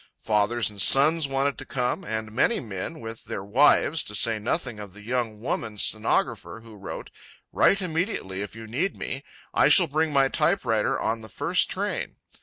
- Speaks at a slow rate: No, average, 180 wpm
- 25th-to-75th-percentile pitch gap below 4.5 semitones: No, average, 4.9 semitones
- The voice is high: No, low, 115 Hz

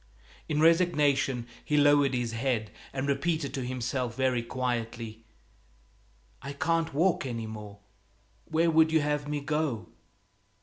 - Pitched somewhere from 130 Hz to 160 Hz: Yes, low, 135 Hz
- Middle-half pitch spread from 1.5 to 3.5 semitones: No, average, 4.0 semitones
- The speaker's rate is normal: No, slow, 130 wpm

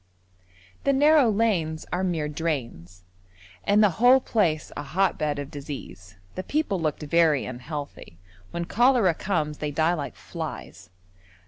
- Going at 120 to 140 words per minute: Yes, slow, 135 wpm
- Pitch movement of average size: No, wide, 5.7 semitones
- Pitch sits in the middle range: Yes, medium, 160 Hz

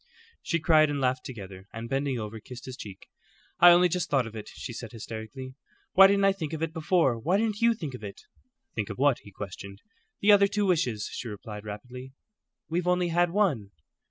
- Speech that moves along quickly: Yes, fast, 210 wpm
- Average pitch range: No, wide, 7.9 semitones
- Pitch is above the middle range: No, low, 135 Hz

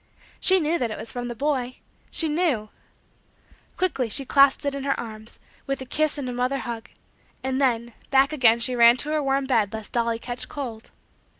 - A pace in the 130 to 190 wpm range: No, average, 200 wpm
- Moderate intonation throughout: Yes, average, 3.2 semitones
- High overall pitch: Yes, very high, 255 Hz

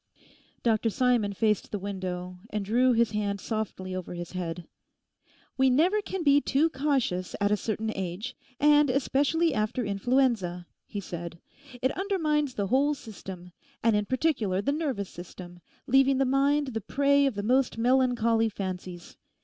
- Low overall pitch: No, high, 225 Hz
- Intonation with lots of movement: Yes, wide, 5.9 semitones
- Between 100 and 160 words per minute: Yes, average, 155 wpm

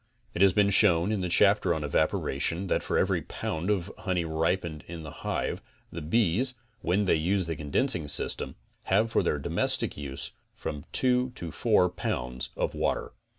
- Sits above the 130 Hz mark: No, very low, 85 Hz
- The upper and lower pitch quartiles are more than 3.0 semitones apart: Yes, average, 4.4 semitones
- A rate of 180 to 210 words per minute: Yes, average, 185 wpm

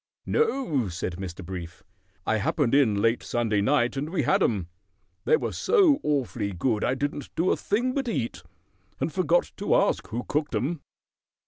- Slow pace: No, average, 175 wpm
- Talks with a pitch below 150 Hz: Yes, low, 135 Hz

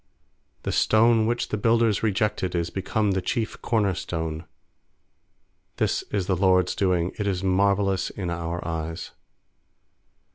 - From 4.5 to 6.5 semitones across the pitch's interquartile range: No, average, 3.3 semitones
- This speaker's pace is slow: Yes, slow, 130 wpm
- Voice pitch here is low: Yes, very low, 95 Hz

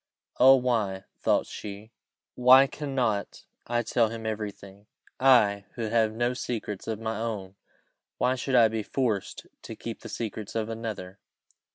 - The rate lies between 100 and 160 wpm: Yes, average, 155 wpm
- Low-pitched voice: Yes, low, 110 Hz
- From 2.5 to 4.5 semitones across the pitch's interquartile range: Yes, average, 2.9 semitones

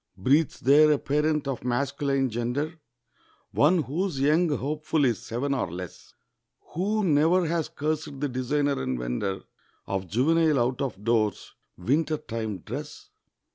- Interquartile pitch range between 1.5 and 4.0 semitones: No, average, 4.5 semitones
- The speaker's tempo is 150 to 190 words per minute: No, slow, 135 wpm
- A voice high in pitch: No, medium, 140 Hz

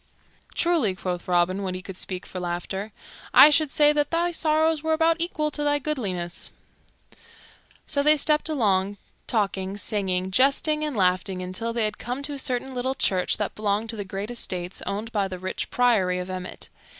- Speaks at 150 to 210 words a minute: Yes, average, 185 wpm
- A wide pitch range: Yes, wide, 7.7 semitones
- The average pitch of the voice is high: Yes, high, 215 Hz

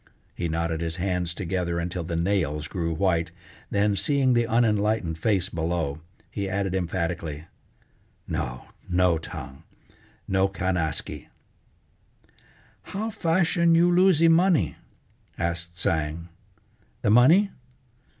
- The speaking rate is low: Yes, slow, 110 wpm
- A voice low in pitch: Yes, very low, 90 Hz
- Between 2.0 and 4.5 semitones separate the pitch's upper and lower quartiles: No, wide, 5.4 semitones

